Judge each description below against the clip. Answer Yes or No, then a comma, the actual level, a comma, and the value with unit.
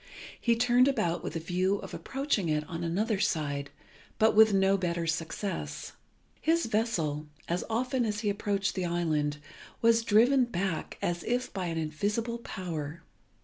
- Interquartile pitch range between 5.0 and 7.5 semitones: Yes, wide, 5.5 semitones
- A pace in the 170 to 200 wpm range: No, average, 155 wpm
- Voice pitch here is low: No, high, 195 Hz